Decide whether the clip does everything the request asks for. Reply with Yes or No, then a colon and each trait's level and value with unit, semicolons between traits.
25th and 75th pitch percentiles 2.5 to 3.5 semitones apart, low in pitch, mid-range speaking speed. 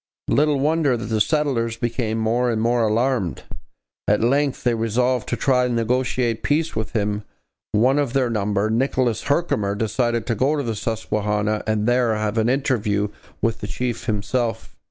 Yes: average, 2.9 semitones; low, 115 Hz; average, 170 wpm